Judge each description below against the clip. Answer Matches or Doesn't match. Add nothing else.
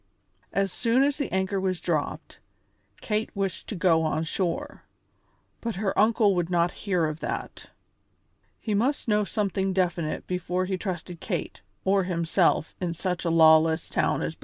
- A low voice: Doesn't match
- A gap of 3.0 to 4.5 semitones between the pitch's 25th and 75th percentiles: Matches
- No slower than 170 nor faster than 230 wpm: Doesn't match